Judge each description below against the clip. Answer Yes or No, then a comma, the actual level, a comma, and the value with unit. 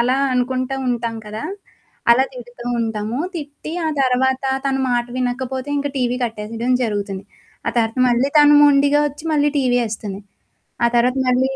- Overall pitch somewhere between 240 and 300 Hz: Yes, very high, 250 Hz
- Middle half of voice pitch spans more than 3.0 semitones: No, narrow, 2.5 semitones